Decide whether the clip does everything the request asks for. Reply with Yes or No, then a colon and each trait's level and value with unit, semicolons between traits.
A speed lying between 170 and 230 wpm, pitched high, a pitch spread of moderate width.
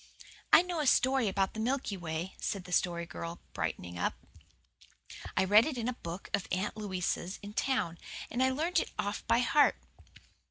No: average, 185 wpm; high, 205 Hz; wide, 6.3 semitones